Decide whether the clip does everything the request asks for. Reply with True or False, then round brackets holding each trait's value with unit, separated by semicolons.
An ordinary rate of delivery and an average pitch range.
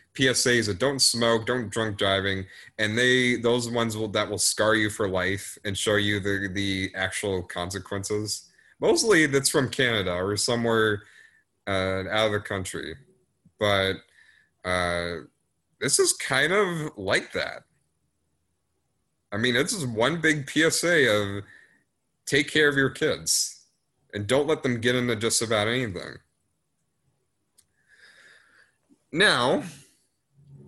False (130 wpm; 4.3 semitones)